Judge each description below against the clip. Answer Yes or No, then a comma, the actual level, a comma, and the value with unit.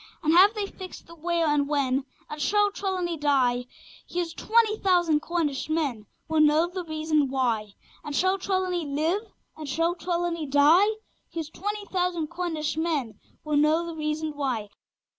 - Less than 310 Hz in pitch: No, very high, 320 Hz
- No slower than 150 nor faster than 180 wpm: Yes, average, 160 wpm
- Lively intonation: No, average, 3.4 semitones